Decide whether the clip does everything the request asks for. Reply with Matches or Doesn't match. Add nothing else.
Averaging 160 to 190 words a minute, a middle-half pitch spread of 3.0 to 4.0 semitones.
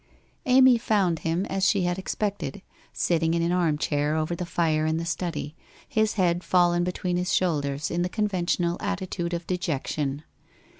Doesn't match